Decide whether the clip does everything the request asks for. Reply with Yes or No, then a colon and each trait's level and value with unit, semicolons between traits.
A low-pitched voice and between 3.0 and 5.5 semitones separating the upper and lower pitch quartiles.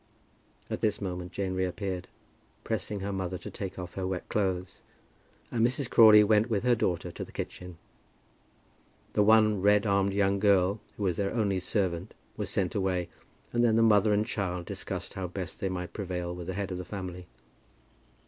No: very low, 95 Hz; narrow, 2.4 semitones